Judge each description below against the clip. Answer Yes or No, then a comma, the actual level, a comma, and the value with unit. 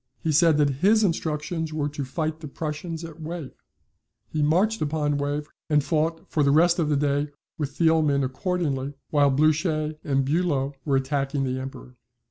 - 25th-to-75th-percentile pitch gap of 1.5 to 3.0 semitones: Yes, narrow, 2.4 semitones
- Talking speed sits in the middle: Yes, average, 170 wpm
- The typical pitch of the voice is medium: Yes, medium, 150 Hz